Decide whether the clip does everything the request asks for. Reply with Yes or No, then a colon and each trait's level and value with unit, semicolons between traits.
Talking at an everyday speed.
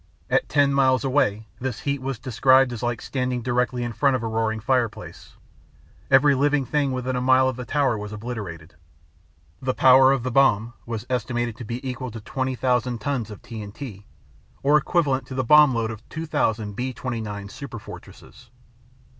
Yes: average, 170 wpm